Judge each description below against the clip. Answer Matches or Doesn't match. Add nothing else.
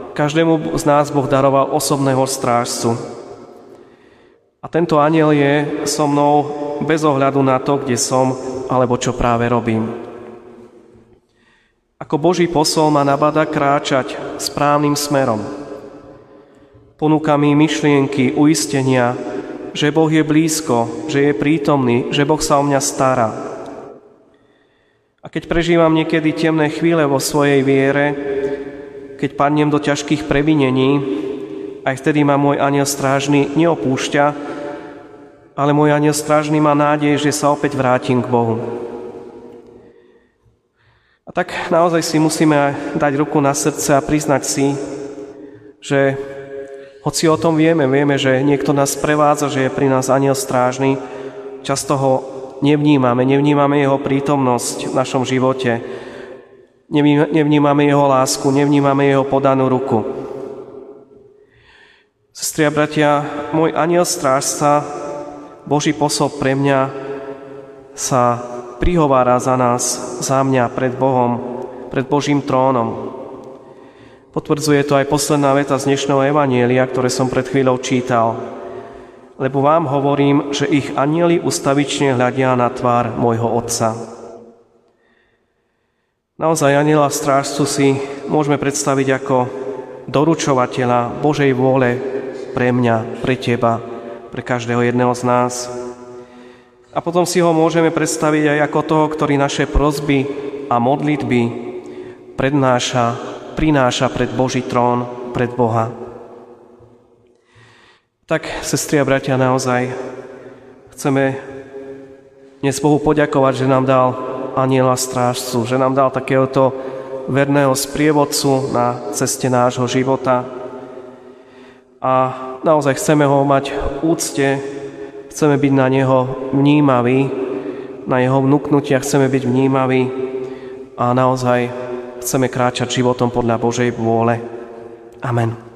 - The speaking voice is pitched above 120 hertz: Matches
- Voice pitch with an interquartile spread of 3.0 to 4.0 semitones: Doesn't match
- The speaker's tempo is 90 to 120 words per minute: Matches